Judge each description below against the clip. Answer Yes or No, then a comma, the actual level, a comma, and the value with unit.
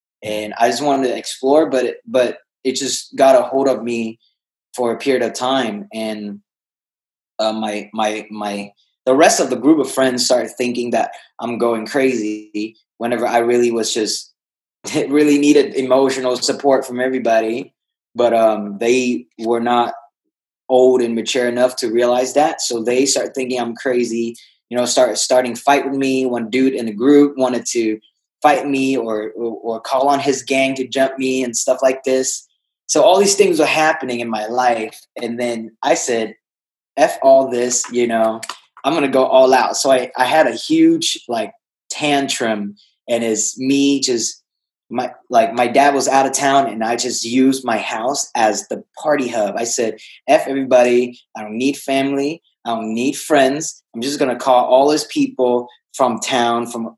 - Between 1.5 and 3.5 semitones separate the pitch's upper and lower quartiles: Yes, average, 2.7 semitones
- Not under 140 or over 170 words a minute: No, average, 180 wpm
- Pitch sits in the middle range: No, low, 125 Hz